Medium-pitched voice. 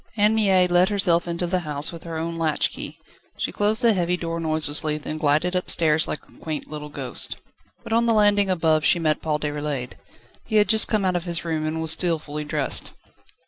Yes: medium, 165 Hz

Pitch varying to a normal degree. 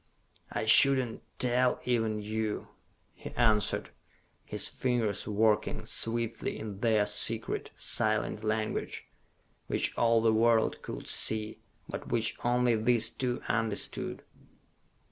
No: narrow, 1.7 semitones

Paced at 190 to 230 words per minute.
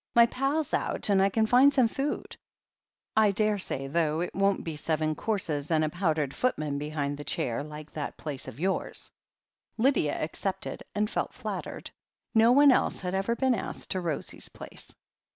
No: average, 175 wpm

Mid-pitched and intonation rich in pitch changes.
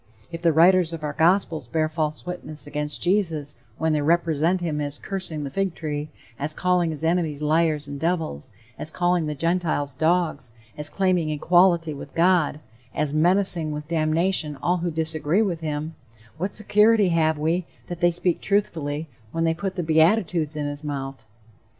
No: medium, 160 Hz; average, 2.8 semitones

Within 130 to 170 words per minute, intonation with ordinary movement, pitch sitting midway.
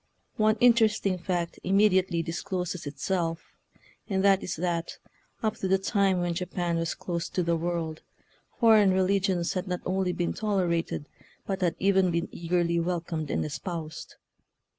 No: average, 150 wpm; narrow, 2.3 semitones; medium, 180 Hz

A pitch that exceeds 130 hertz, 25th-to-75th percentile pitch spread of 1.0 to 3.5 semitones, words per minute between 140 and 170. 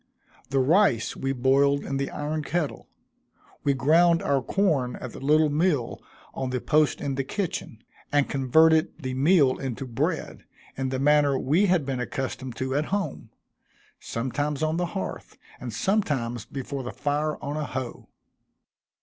Yes: medium, 140 Hz; average, 3.0 semitones; average, 160 wpm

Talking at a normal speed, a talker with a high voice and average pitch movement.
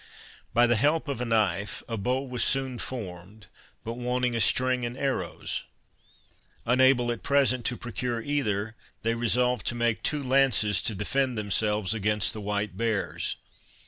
No: average, 155 wpm; low, 120 Hz; average, 3.1 semitones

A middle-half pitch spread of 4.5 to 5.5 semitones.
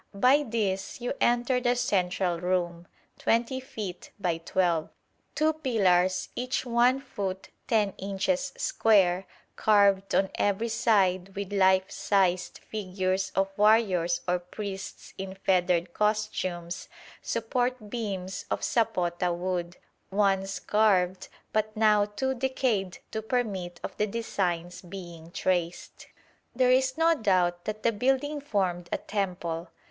No: average, 4.0 semitones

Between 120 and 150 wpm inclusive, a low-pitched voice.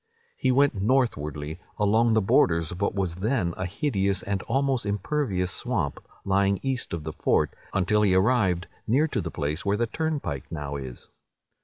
No: average, 170 wpm; low, 100 Hz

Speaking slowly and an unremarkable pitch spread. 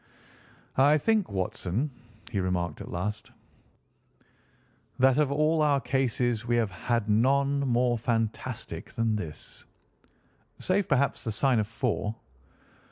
Yes: slow, 120 wpm; average, 4.7 semitones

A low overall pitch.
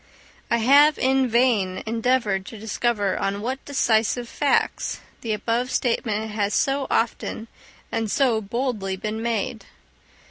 No: high, 230 Hz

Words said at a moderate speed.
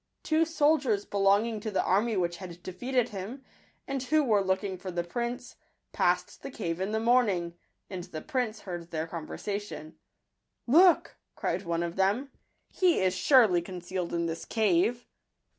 Yes: average, 170 wpm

